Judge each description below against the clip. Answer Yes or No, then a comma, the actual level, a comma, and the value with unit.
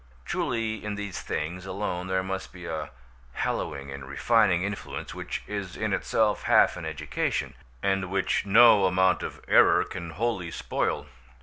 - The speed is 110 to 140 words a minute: No, average, 150 wpm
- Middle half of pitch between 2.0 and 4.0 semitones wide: Yes, average, 2.8 semitones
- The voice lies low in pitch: Yes, very low, 95 Hz